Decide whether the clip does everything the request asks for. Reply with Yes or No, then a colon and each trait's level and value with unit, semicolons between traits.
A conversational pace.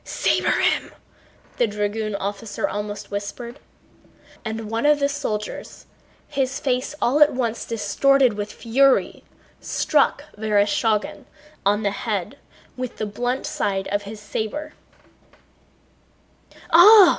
No: slow, 115 wpm